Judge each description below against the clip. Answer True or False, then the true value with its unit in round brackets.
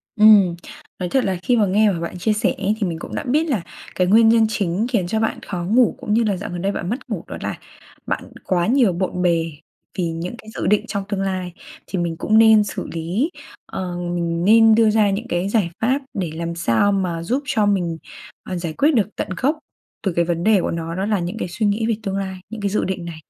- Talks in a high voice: True (195 Hz)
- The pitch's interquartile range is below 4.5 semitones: True (3.9 semitones)